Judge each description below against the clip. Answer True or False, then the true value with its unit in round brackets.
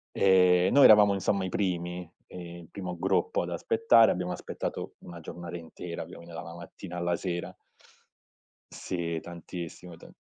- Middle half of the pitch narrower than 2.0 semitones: True (1.6 semitones)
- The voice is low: True (90 Hz)